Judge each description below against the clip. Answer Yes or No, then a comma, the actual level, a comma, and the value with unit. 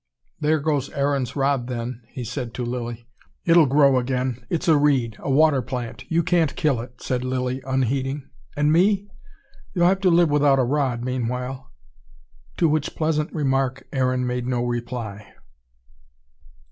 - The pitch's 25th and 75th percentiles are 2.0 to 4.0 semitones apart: Yes, average, 3.1 semitones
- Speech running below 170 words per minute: Yes, average, 155 wpm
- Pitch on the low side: Yes, low, 130 Hz